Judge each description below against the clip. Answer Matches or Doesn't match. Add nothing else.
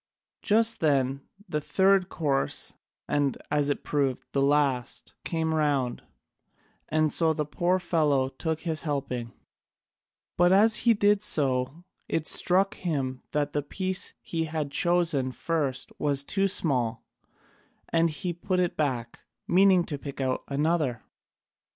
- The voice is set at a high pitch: Doesn't match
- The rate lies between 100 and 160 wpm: Matches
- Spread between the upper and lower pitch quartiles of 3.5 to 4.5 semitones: Matches